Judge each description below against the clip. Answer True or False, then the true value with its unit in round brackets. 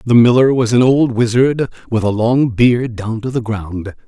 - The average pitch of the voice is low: True (120 Hz)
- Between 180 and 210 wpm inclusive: True (205 wpm)